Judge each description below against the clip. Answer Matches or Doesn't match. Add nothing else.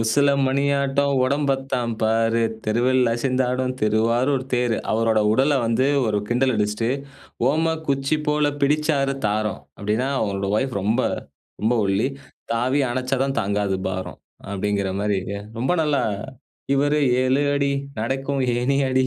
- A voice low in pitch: Matches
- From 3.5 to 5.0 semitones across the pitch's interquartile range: Matches